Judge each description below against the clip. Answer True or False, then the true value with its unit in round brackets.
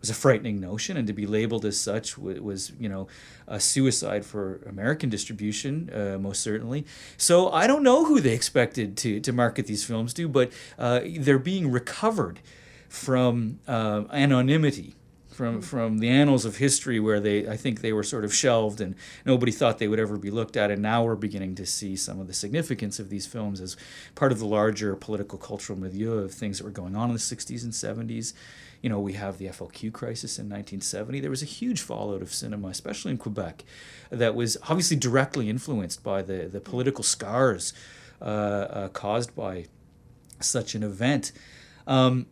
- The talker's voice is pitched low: True (115 Hz)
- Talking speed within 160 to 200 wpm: True (190 wpm)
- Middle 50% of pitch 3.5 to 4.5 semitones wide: True (4.2 semitones)